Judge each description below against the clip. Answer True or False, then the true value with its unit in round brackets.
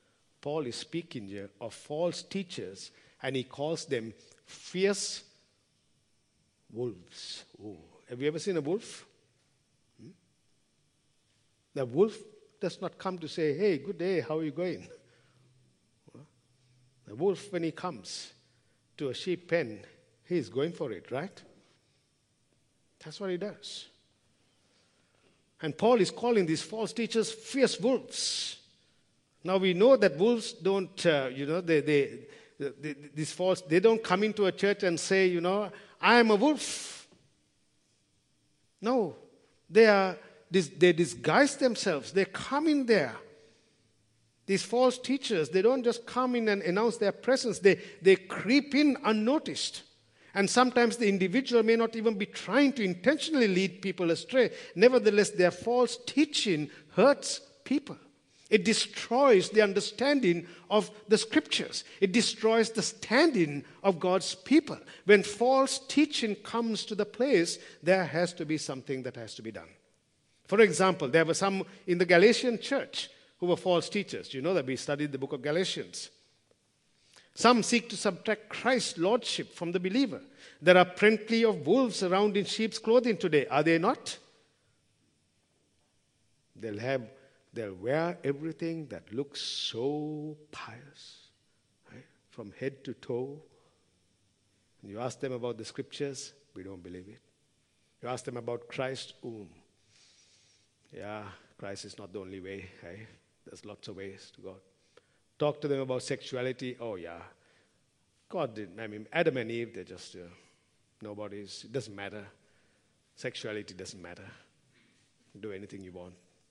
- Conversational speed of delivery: True (150 wpm)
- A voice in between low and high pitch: True (170 Hz)